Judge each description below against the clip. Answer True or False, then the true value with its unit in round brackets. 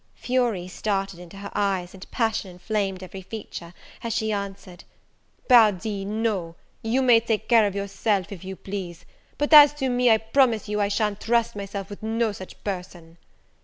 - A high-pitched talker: True (205 Hz)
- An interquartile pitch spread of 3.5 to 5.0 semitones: False (2.9 semitones)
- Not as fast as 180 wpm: True (170 wpm)